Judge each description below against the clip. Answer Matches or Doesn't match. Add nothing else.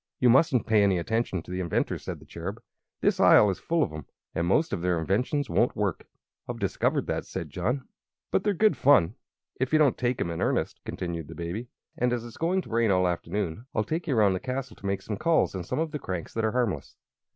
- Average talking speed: Doesn't match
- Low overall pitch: Matches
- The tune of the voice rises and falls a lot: Matches